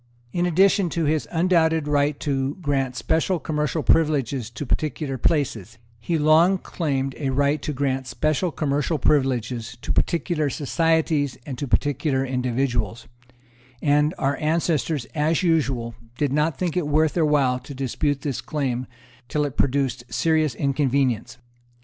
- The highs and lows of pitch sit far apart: No, average, 3.0 semitones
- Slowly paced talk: No, average, 145 wpm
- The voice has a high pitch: No, medium, 145 Hz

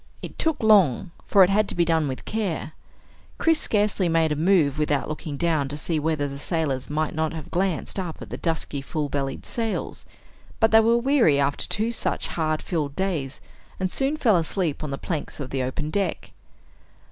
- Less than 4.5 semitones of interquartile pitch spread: No, average, 5.2 semitones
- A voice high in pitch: No, medium, 160 Hz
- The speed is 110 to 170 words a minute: No, average, 195 wpm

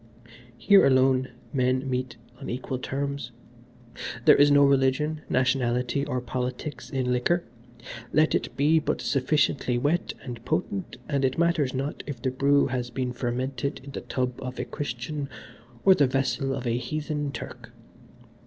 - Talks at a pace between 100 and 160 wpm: Yes, average, 155 wpm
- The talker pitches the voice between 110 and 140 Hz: Yes, low, 135 Hz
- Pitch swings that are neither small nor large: No, narrow, 2.3 semitones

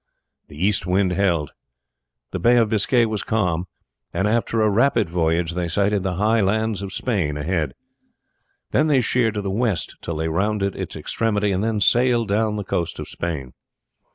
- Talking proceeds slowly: No, average, 180 wpm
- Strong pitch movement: No, average, 4.2 semitones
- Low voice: Yes, low, 100 Hz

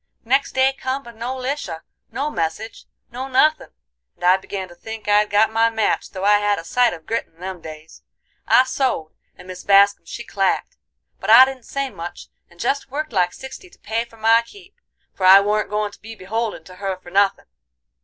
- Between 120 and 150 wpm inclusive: No, fast, 205 wpm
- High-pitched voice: Yes, high, 215 Hz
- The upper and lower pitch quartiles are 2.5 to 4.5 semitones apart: No, average, 5.2 semitones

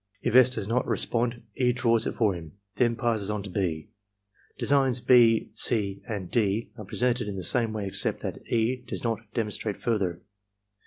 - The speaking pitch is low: Yes, low, 115 Hz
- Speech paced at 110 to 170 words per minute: No, average, 190 wpm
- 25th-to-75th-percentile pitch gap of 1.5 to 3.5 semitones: Yes, average, 3.2 semitones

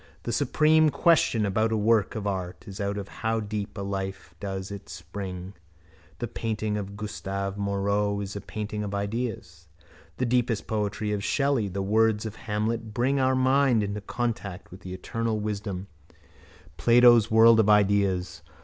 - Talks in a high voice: No, low, 105 Hz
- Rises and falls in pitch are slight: Yes, narrow, 2.3 semitones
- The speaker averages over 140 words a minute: Yes, average, 160 wpm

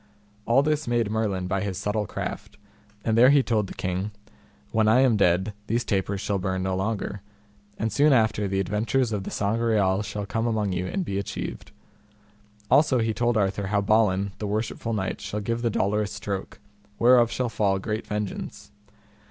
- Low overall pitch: Yes, low, 105 Hz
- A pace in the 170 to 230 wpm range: Yes, average, 180 wpm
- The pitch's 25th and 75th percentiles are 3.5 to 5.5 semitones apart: No, average, 2.9 semitones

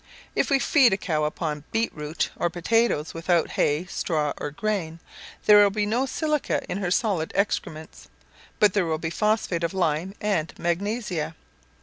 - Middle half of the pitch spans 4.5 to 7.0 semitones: Yes, average, 4.9 semitones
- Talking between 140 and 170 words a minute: Yes, average, 160 wpm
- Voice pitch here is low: No, medium, 180 Hz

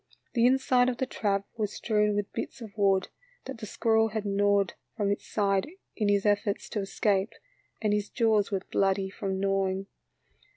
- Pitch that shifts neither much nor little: No, narrow, 2.0 semitones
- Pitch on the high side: Yes, high, 205 Hz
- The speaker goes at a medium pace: Yes, average, 175 wpm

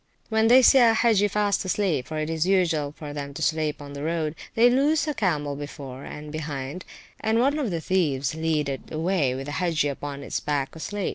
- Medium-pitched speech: Yes, medium, 160 Hz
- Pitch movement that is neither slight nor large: No, wide, 6.0 semitones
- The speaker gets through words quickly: Yes, fast, 215 wpm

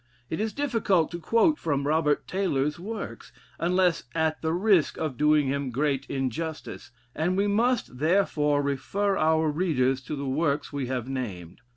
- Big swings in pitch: No, average, 4.8 semitones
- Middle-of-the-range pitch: Yes, medium, 155 Hz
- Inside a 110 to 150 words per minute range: No, average, 160 wpm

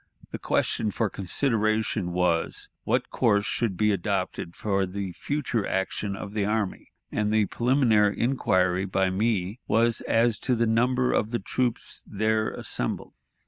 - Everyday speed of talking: Yes, average, 145 wpm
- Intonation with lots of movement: No, average, 3.1 semitones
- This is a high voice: No, low, 105 Hz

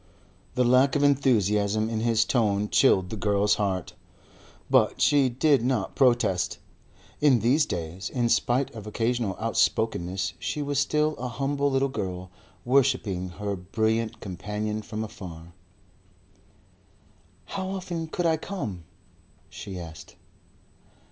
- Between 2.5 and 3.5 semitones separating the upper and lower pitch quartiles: No, wide, 5.4 semitones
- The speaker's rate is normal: No, slow, 125 wpm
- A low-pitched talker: Yes, low, 110 Hz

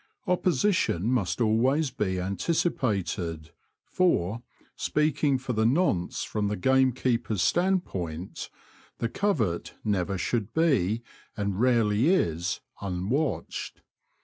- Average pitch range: No, wide, 6.8 semitones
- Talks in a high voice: No, low, 115 Hz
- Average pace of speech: No, slow, 120 wpm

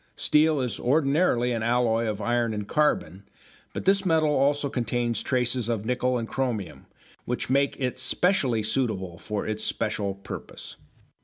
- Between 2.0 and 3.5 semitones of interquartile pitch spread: No, average, 3.9 semitones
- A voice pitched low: Yes, low, 120 Hz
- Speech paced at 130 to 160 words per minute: Yes, average, 150 wpm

